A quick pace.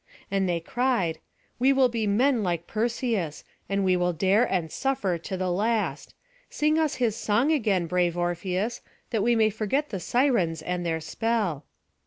No: average, 170 wpm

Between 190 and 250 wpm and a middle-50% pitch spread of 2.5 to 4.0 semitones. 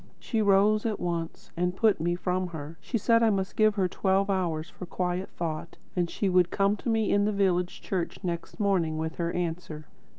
Yes: fast, 205 wpm; average, 2.8 semitones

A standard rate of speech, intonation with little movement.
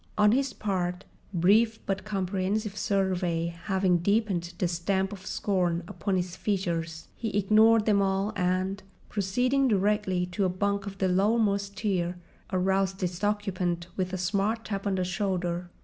Yes: average, 150 wpm; narrow, 2.3 semitones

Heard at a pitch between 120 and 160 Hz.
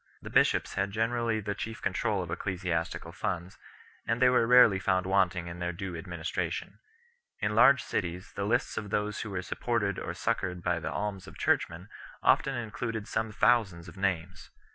No: low, 100 Hz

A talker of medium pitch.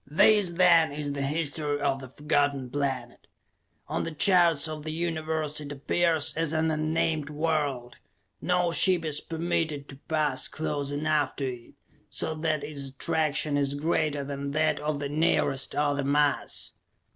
Yes: medium, 150 Hz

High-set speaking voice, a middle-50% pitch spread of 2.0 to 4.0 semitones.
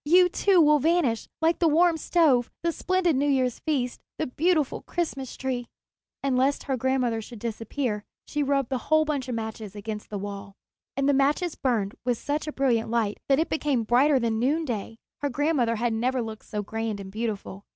No: very high, 260 Hz; average, 4.9 semitones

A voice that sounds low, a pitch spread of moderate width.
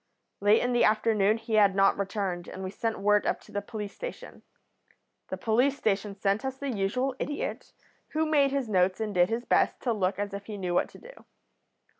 No: high, 210 Hz; average, 3.9 semitones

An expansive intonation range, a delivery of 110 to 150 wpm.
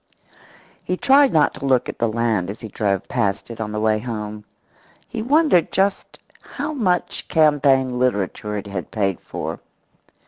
No: wide, 8.8 semitones; average, 165 wpm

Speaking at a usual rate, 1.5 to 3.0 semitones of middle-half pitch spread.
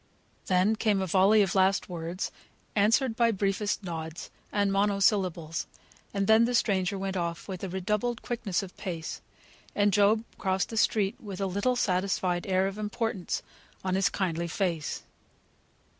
Yes: average, 150 wpm; narrow, 2.4 semitones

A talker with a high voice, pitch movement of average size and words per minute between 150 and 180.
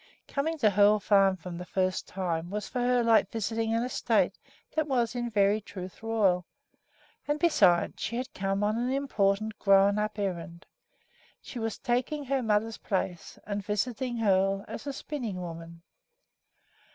Yes: high, 210 Hz; average, 3.7 semitones; average, 160 wpm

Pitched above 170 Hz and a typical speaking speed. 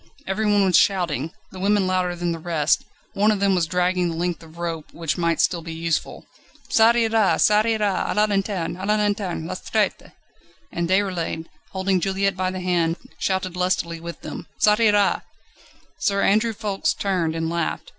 Yes: medium, 185 Hz; average, 180 wpm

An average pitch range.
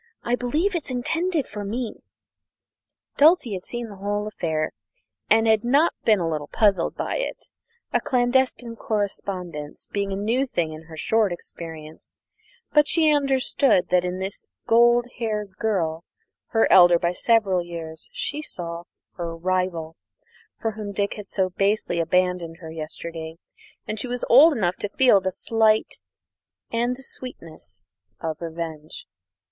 No: wide, 6.0 semitones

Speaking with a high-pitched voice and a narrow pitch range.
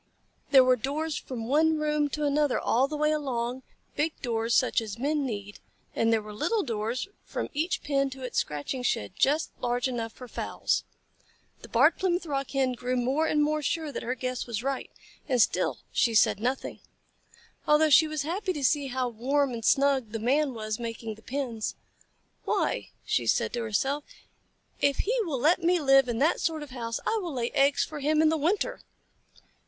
No: very high, 270 Hz; average, 4.0 semitones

